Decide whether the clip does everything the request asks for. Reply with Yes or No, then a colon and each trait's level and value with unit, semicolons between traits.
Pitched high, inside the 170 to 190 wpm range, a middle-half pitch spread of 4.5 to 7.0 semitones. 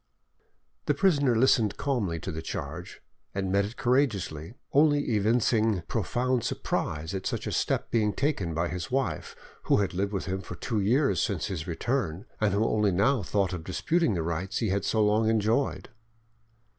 No: low, 105 Hz; average, 175 wpm; average, 4.8 semitones